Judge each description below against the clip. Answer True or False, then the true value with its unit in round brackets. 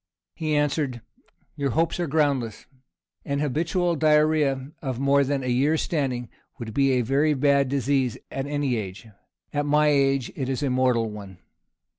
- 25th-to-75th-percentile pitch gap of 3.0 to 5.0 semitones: False (2.6 semitones)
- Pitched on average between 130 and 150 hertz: True (140 Hz)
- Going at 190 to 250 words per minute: False (160 wpm)